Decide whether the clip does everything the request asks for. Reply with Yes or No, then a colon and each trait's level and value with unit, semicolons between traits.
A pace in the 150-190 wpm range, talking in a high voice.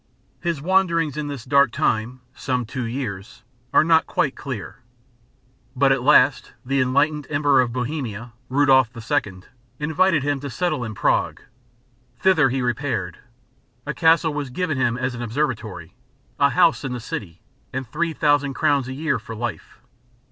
No: average, 155 wpm; low, 135 Hz